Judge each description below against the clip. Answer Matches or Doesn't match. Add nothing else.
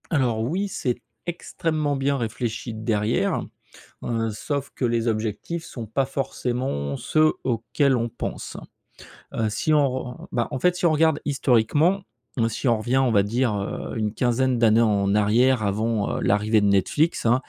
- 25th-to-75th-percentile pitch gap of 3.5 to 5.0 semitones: Matches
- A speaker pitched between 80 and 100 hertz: Doesn't match